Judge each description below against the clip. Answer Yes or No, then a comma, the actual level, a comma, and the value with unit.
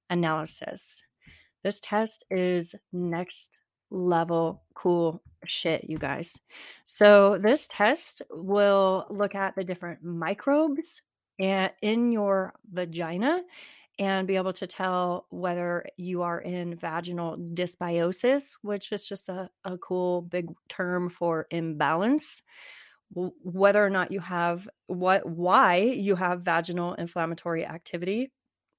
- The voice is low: No, medium, 185 Hz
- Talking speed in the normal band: No, slow, 115 wpm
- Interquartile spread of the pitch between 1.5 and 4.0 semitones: Yes, average, 2.9 semitones